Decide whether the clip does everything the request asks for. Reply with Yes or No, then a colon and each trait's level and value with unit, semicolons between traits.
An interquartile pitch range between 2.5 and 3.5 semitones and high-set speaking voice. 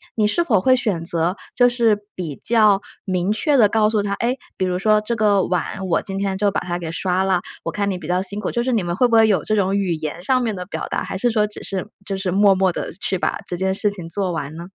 Yes: average, 3.0 semitones; high, 195 Hz